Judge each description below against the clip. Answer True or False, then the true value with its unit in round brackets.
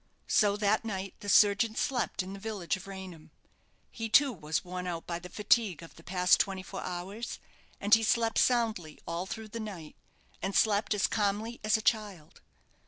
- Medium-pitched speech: False (200 Hz)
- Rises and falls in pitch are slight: False (3.3 semitones)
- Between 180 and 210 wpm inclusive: True (185 wpm)